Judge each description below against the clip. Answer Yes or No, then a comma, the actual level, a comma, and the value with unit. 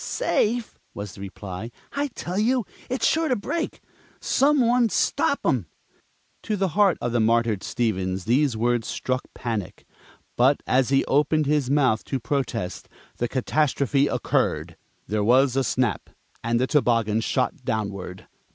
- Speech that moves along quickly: No, average, 150 wpm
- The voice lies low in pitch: Yes, low, 130 Hz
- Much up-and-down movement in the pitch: Yes, wide, 5.8 semitones